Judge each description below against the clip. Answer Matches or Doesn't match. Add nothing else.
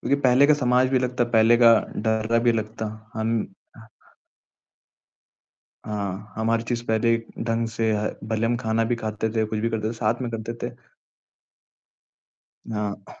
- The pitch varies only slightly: Matches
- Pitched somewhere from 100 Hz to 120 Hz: Matches